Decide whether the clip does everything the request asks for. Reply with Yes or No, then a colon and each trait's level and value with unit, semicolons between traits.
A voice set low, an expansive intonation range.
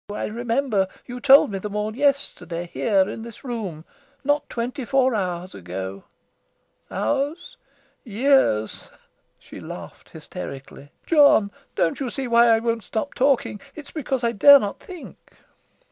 No: high, 235 Hz; wide, 5.8 semitones